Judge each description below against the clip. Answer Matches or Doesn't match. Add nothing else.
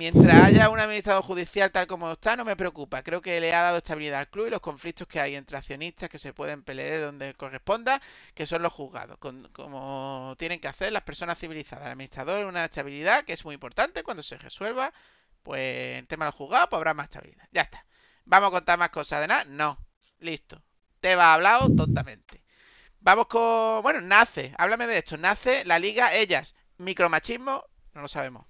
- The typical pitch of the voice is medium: Matches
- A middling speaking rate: Doesn't match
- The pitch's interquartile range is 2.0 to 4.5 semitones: Doesn't match